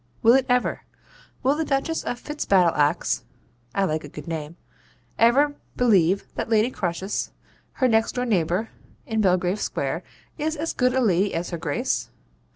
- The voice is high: Yes, high, 220 Hz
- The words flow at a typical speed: Yes, average, 160 wpm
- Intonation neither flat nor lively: No, wide, 6.3 semitones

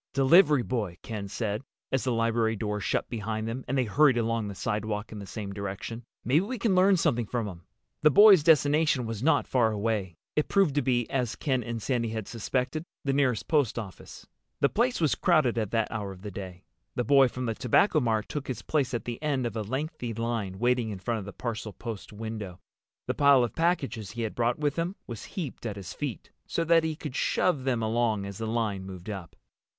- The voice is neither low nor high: No, low, 120 Hz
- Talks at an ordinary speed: No, fast, 215 wpm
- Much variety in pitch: No, average, 4.7 semitones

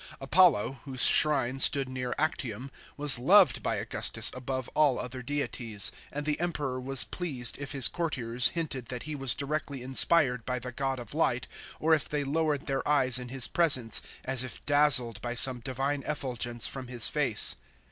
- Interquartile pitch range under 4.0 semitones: Yes, average, 2.8 semitones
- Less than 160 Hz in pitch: Yes, low, 135 Hz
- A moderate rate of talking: Yes, average, 175 wpm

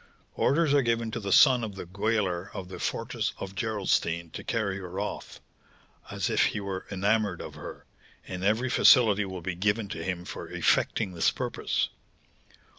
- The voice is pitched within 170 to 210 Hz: No, low, 100 Hz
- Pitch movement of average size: Yes, average, 3.2 semitones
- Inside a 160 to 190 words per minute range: Yes, average, 175 wpm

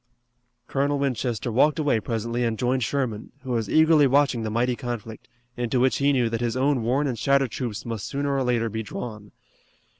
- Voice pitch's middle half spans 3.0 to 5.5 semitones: Yes, average, 3.3 semitones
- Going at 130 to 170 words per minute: No, average, 190 wpm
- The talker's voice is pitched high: No, low, 125 Hz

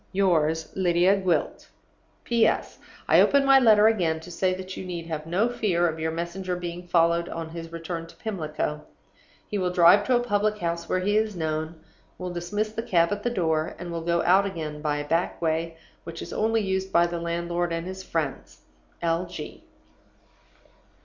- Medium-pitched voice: Yes, medium, 175 Hz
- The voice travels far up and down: No, average, 2.7 semitones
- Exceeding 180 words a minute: Yes, average, 190 wpm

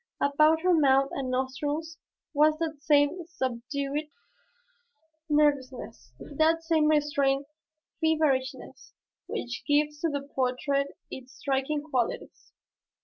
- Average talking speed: No, slow, 100 wpm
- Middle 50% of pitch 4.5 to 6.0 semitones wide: No, narrow, 2.5 semitones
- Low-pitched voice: No, very high, 290 Hz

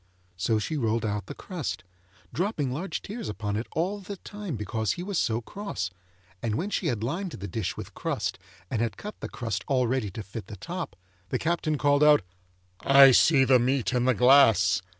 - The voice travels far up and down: Yes, wide, 7.2 semitones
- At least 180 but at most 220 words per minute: Yes, average, 200 wpm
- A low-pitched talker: Yes, low, 130 Hz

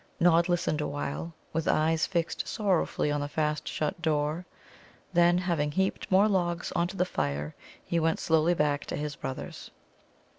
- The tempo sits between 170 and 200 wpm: No, average, 160 wpm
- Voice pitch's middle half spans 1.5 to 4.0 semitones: Yes, average, 2.8 semitones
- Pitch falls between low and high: Yes, medium, 165 Hz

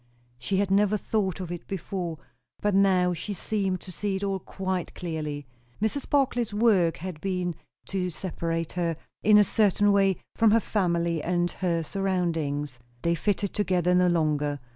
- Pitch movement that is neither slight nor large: Yes, average, 3.0 semitones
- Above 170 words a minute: No, average, 165 wpm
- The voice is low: No, medium, 185 Hz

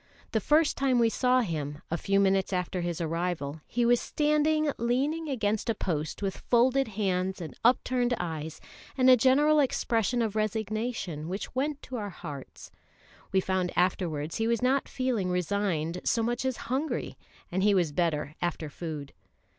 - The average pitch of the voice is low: No, high, 205 Hz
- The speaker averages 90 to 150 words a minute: No, average, 165 wpm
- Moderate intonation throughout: No, wide, 6.4 semitones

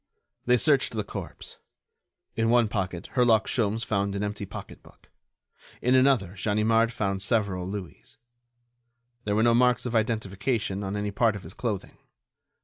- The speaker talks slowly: No, average, 145 wpm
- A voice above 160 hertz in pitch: No, low, 105 Hz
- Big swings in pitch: No, average, 2.9 semitones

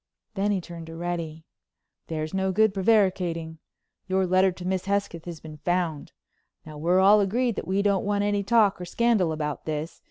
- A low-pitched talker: No, medium, 185 Hz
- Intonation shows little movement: No, average, 3.5 semitones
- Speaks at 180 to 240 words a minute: Yes, average, 185 wpm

